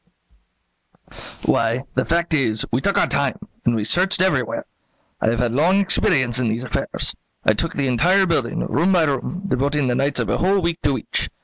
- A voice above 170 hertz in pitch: No, medium, 140 Hz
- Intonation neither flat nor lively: No, wide, 6.0 semitones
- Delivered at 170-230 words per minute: Yes, average, 195 wpm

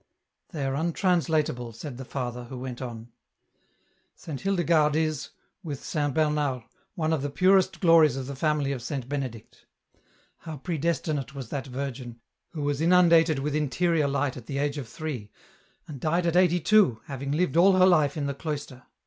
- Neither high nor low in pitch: Yes, medium, 145 Hz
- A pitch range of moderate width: Yes, average, 3.5 semitones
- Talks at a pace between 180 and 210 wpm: Yes, average, 185 wpm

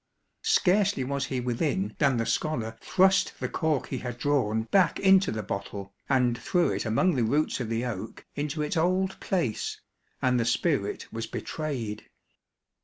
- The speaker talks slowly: No, average, 165 wpm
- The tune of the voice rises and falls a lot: Yes, wide, 6.3 semitones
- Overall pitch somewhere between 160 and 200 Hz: No, low, 135 Hz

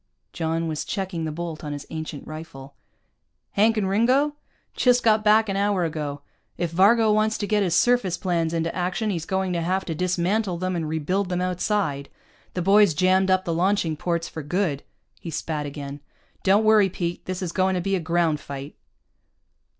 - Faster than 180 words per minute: Yes, average, 190 wpm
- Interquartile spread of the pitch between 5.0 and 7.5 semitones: No, average, 3.7 semitones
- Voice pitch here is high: No, medium, 180 Hz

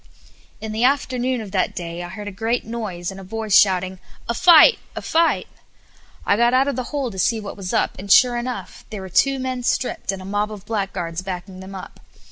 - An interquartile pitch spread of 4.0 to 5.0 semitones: Yes, average, 4.5 semitones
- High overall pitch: Yes, high, 210 Hz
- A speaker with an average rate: No, fast, 225 wpm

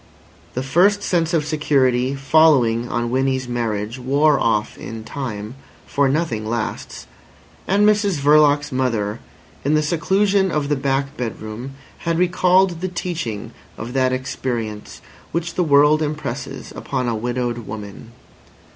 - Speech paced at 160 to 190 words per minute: No, slow, 135 wpm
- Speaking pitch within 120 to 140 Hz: Yes, low, 135 Hz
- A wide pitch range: No, average, 4.9 semitones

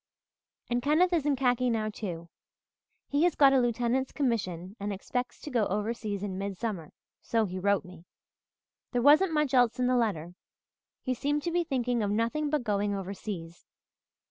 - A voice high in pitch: Yes, high, 235 Hz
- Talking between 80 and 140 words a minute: No, average, 170 wpm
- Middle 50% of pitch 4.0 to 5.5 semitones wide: Yes, average, 5.0 semitones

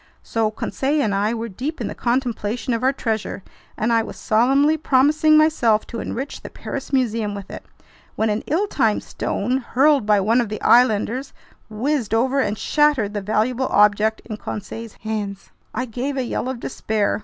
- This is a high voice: Yes, high, 230 Hz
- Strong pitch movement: No, average, 3.8 semitones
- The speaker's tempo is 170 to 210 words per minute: Yes, average, 180 wpm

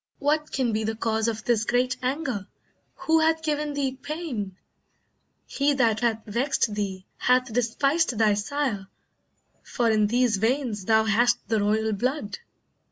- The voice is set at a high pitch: Yes, high, 235 Hz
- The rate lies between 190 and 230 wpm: No, average, 150 wpm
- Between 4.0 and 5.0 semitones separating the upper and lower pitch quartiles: Yes, average, 4.3 semitones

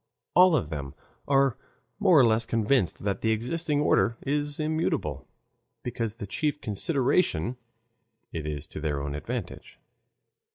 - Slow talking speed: Yes, slow, 130 wpm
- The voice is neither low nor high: No, low, 120 Hz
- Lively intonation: Yes, wide, 7.4 semitones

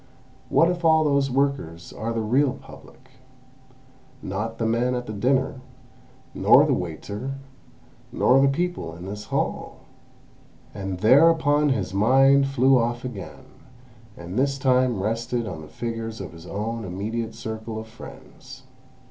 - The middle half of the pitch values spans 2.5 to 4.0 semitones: No, average, 4.4 semitones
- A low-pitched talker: Yes, low, 115 Hz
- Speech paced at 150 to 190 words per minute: No, average, 140 wpm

